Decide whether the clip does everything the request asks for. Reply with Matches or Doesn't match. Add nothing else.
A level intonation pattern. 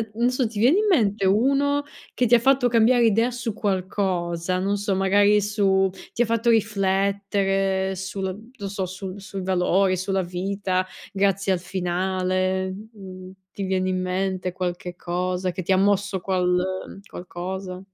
Matches